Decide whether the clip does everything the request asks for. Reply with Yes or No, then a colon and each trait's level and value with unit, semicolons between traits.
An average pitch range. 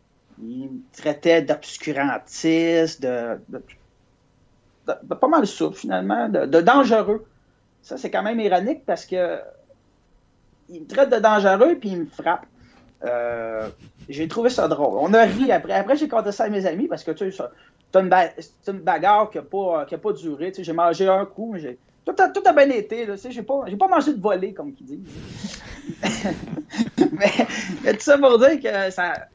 No: wide, 7.6 semitones